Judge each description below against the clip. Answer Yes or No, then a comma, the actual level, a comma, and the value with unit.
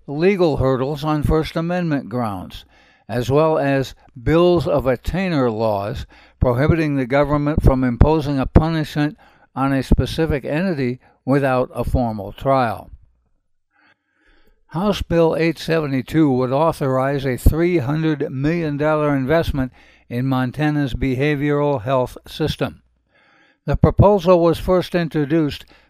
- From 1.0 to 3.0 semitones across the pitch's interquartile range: No, average, 3.6 semitones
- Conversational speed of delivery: No, slow, 110 wpm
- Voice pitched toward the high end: No, medium, 145 Hz